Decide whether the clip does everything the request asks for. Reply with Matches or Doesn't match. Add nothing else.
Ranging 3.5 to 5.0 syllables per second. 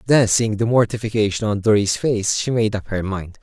Doesn't match